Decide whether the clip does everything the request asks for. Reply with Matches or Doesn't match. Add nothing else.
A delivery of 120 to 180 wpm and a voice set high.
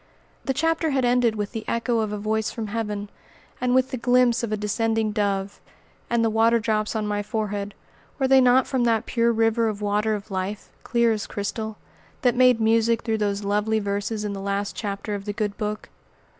Doesn't match